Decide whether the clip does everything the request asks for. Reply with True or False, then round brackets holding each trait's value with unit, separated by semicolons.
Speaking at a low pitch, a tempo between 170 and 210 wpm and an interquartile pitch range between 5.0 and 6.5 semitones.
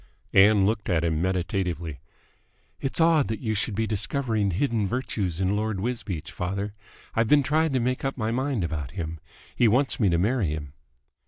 True (105 Hz; 180 wpm; 5.5 semitones)